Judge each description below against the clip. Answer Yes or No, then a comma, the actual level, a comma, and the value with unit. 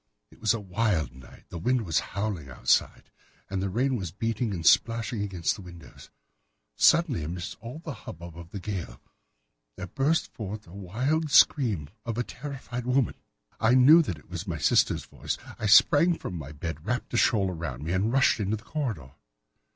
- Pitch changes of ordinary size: No, wide, 6.4 semitones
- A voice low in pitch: Yes, low, 105 Hz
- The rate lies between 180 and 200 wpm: Yes, average, 185 wpm